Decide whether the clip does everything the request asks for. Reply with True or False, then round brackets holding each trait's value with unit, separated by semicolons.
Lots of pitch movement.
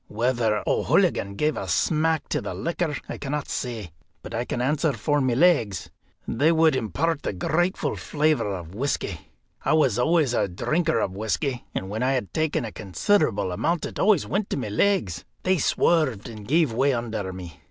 True (6.7 semitones)